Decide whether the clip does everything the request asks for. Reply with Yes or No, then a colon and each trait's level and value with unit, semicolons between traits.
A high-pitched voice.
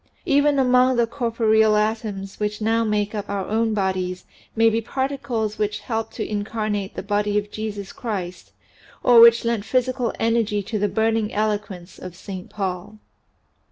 Yes: high, 215 Hz